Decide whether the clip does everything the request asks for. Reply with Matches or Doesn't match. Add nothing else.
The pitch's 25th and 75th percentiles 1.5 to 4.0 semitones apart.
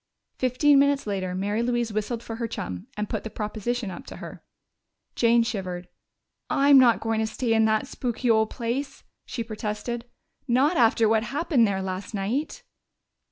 Matches